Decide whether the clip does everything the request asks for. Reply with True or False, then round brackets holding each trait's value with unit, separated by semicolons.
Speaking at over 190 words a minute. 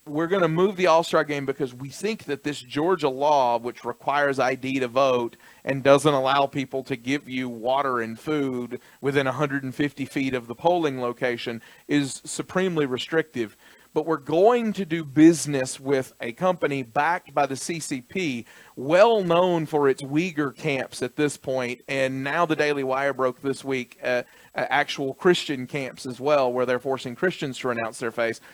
False (175 wpm)